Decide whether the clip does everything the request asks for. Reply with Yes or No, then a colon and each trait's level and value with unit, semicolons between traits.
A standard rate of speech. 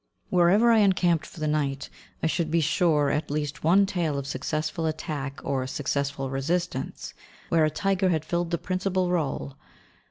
Yes: average, 170 wpm